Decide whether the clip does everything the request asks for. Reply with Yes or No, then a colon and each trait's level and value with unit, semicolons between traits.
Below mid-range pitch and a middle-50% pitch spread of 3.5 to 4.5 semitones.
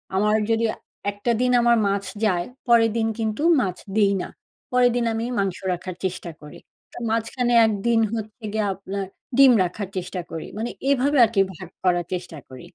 No: high, 210 Hz; average, 3.9 semitones